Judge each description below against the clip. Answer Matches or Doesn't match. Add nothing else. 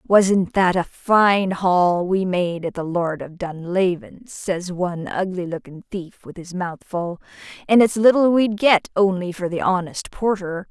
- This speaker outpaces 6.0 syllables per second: Doesn't match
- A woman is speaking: Matches